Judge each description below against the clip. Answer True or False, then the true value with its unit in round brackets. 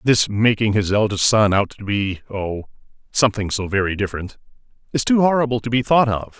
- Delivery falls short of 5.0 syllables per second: False (5.5 syllables/s)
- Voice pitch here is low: True (110 Hz)